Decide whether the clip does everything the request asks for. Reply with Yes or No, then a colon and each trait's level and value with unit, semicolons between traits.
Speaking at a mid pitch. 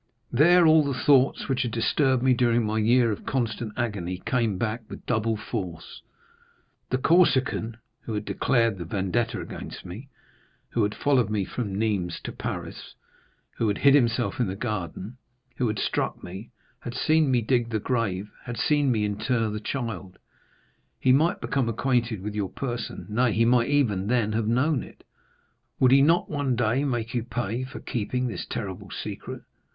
No: low, 115 Hz